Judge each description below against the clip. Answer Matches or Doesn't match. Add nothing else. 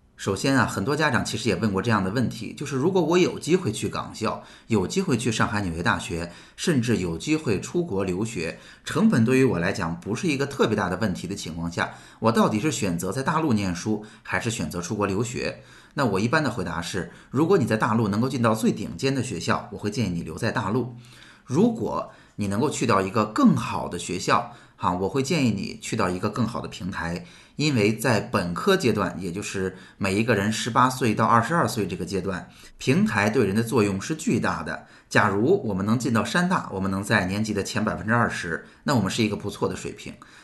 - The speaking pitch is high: Doesn't match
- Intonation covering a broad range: Doesn't match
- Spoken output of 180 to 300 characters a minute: Doesn't match